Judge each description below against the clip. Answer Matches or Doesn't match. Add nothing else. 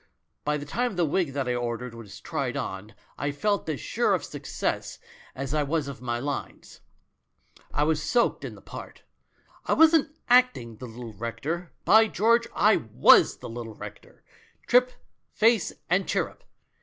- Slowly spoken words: Doesn't match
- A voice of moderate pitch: Matches